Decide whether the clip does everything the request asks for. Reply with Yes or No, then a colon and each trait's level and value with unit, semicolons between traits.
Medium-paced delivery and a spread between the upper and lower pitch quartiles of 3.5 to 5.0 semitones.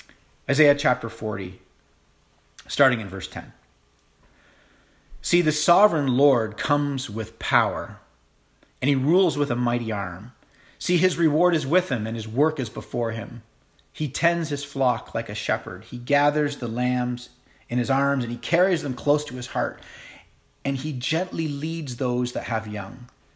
Yes: average, 160 wpm; average, 4.3 semitones